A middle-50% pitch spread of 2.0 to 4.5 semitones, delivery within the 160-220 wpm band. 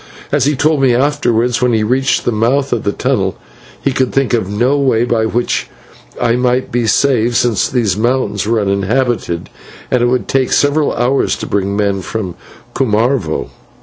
Yes: average, 3.5 semitones; average, 180 wpm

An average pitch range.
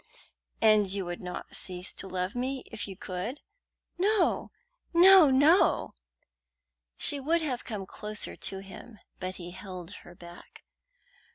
No: wide, 6.5 semitones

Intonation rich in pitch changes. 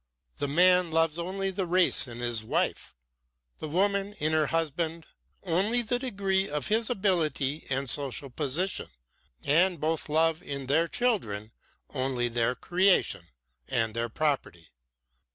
Yes: wide, 5.7 semitones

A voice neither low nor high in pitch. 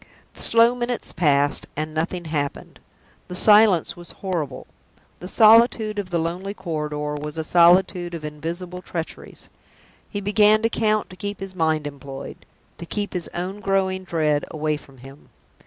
Yes: medium, 175 Hz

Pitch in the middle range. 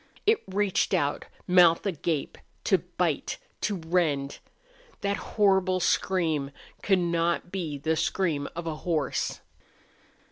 Yes: medium, 170 Hz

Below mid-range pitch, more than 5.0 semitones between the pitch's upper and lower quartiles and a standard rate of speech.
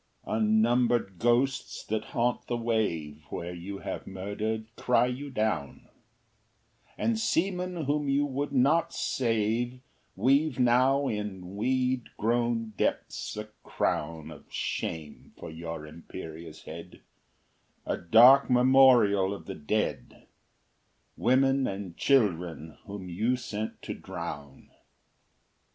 No: low, 110 Hz; wide, 5.4 semitones; slow, 115 wpm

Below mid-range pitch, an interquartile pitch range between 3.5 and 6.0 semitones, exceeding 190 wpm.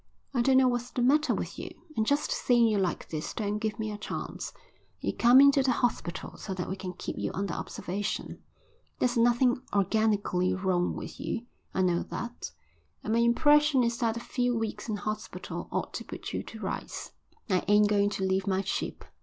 No: high, 220 Hz; average, 4.0 semitones; average, 200 wpm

